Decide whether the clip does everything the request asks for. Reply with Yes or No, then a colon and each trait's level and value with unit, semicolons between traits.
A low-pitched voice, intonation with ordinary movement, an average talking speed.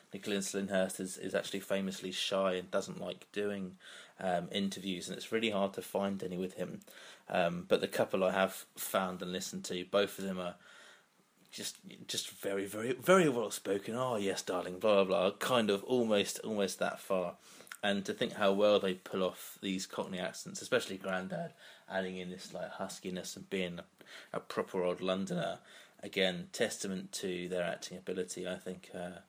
No: very low, 95 Hz; narrow, 1.4 semitones; average, 180 wpm